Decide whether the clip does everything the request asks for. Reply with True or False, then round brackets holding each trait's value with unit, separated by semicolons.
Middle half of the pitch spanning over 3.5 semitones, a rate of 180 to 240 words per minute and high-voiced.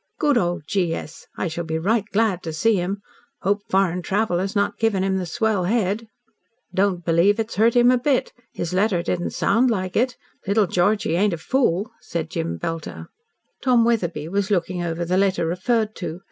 True (4.2 semitones; 190 wpm; 195 Hz)